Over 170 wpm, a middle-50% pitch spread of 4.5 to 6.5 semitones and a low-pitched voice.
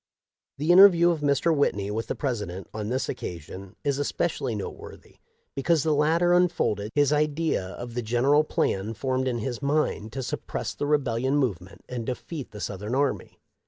Yes: average, 180 wpm; wide, 5.4 semitones; low, 130 Hz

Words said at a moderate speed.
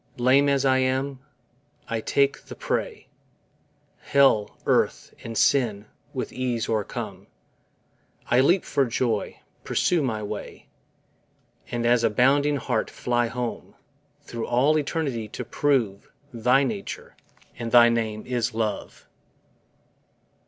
No: slow, 120 wpm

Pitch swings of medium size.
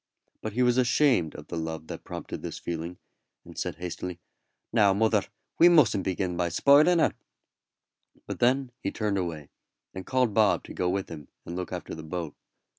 No: wide, 6.1 semitones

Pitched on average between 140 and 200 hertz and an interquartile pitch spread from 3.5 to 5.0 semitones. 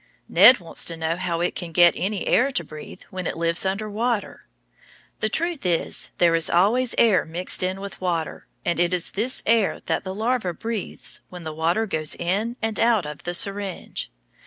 Yes: medium, 185 Hz; average, 4.2 semitones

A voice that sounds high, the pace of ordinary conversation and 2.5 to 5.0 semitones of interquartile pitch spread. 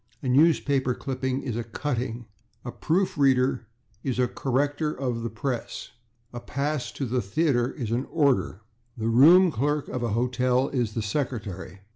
No: low, 125 Hz; average, 160 wpm; average, 3.0 semitones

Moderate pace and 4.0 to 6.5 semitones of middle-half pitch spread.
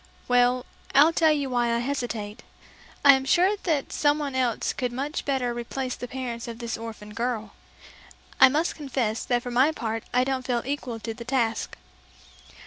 No: average, 170 wpm; average, 2.8 semitones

